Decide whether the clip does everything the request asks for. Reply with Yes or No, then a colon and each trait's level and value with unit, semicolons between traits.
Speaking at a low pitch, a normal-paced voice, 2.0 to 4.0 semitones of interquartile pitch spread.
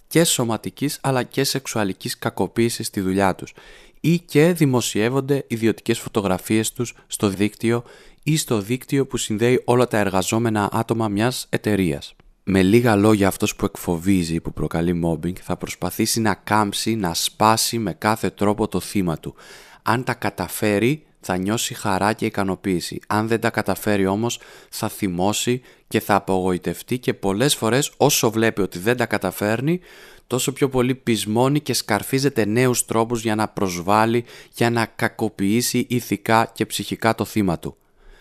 Yes: low, 110 Hz; average, 150 wpm; average, 3.7 semitones